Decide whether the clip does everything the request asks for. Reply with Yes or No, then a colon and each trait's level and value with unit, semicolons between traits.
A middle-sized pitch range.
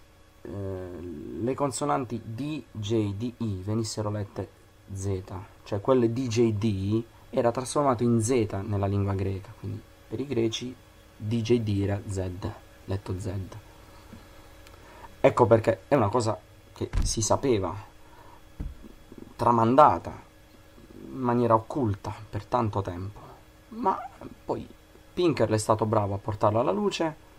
Yes: average, 3.1 semitones